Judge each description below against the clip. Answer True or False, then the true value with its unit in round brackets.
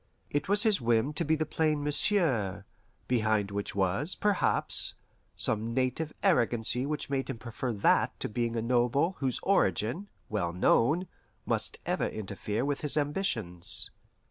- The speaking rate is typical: True (145 wpm)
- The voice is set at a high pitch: False (125 Hz)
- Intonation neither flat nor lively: False (5.7 semitones)